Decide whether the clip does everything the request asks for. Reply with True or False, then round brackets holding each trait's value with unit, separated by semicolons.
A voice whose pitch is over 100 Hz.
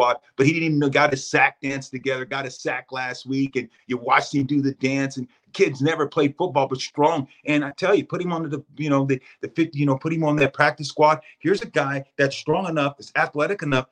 True (140 Hz)